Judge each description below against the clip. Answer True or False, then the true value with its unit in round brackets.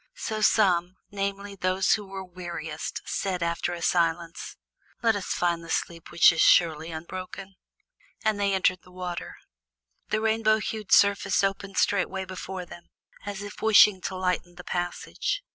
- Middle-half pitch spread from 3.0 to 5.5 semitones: False (2.6 semitones)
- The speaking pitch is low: False (185 Hz)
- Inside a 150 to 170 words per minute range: True (155 wpm)